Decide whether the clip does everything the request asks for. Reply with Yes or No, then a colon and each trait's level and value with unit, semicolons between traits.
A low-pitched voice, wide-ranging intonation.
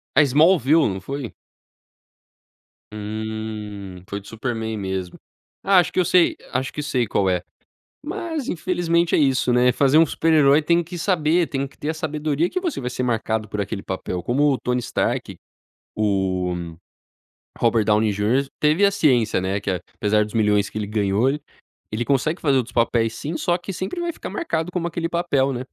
Yes: low, 130 Hz; wide, 7.2 semitones